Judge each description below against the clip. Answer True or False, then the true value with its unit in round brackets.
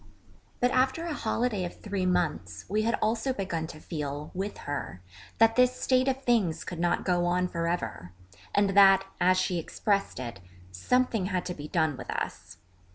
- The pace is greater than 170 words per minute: True (180 wpm)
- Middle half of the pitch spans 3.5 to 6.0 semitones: True (5.1 semitones)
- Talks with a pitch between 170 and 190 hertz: True (185 Hz)